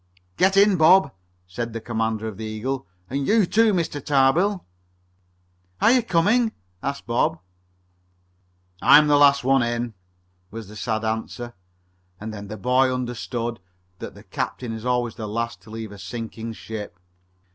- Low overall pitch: Yes, low, 120 Hz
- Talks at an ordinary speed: Yes, average, 155 wpm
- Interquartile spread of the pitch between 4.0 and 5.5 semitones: Yes, average, 5.0 semitones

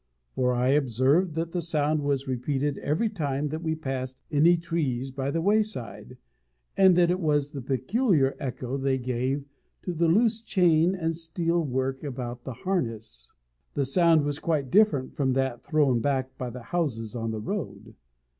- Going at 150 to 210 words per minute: Yes, average, 170 wpm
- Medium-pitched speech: Yes, medium, 145 Hz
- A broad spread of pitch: No, average, 4.5 semitones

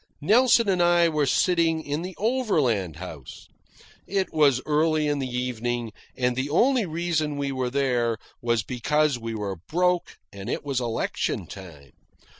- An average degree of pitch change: No, wide, 6.1 semitones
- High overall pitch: No, medium, 140 Hz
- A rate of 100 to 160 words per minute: Yes, average, 155 wpm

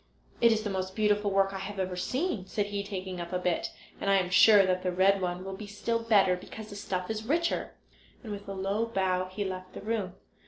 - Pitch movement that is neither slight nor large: No, narrow, 2.3 semitones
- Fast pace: Yes, fast, 240 wpm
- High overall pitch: Yes, high, 195 Hz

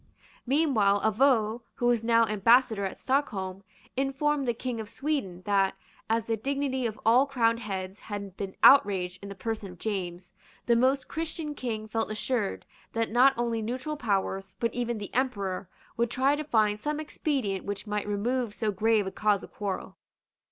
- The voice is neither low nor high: No, high, 225 Hz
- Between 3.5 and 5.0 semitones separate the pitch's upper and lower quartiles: Yes, average, 4.3 semitones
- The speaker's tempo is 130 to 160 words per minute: No, average, 175 wpm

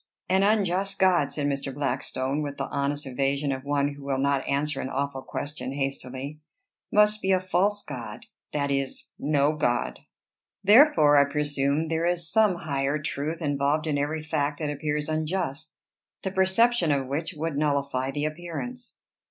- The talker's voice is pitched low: No, medium, 145 Hz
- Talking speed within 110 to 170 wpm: Yes, average, 160 wpm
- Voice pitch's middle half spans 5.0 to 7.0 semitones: No, average, 3.3 semitones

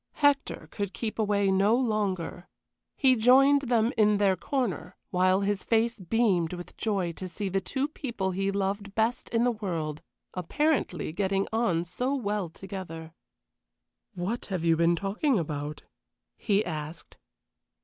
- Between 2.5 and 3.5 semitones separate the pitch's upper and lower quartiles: No, average, 4.4 semitones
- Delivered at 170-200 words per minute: No, average, 145 wpm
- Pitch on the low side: No, high, 200 Hz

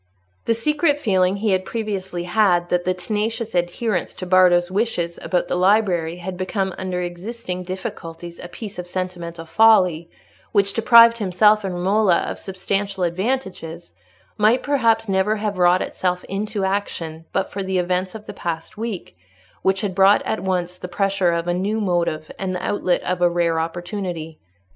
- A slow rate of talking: No, average, 165 wpm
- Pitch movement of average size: Yes, average, 3.0 semitones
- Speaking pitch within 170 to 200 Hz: Yes, medium, 185 Hz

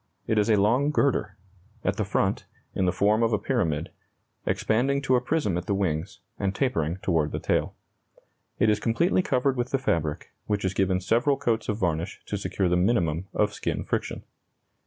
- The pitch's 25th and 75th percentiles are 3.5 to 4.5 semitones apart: No, average, 5.2 semitones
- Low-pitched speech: Yes, low, 105 Hz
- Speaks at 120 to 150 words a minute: No, average, 190 wpm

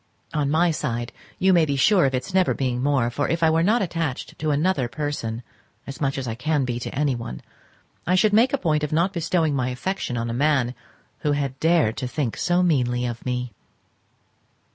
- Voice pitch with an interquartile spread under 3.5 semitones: No, average, 5.0 semitones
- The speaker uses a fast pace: Yes, fast, 210 wpm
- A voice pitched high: No, medium, 145 Hz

